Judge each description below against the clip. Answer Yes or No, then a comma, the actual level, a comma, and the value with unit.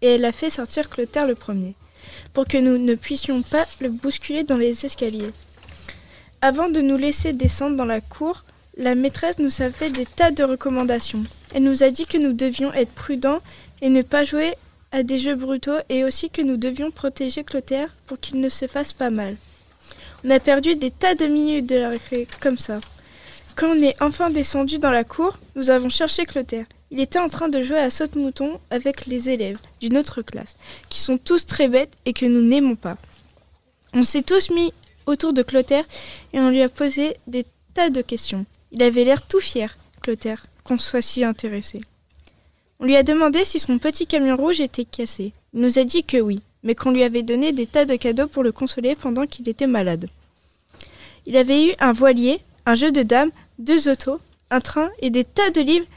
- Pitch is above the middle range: Yes, very high, 265 Hz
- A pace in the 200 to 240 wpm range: Yes, average, 205 wpm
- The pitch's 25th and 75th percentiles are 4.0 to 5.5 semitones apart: No, average, 3.1 semitones